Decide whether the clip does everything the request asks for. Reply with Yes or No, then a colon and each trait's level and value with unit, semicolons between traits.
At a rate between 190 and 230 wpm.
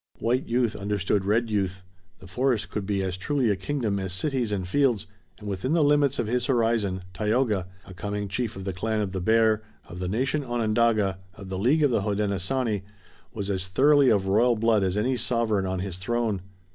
Yes: average, 200 wpm